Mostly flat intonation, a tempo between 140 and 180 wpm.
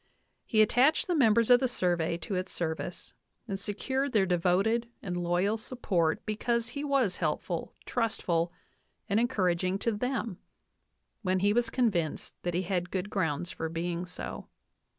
No: average, 4.9 semitones; average, 155 wpm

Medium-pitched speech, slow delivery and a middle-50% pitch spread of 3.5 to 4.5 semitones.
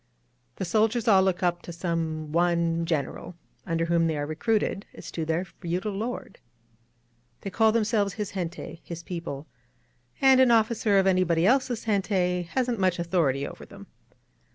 No: medium, 180 Hz; average, 165 wpm; average, 4.2 semitones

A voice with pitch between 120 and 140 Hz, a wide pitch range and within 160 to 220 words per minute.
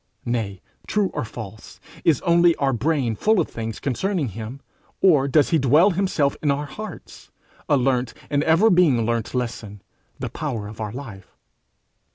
Yes: low, 135 Hz; wide, 6.2 semitones; average, 165 wpm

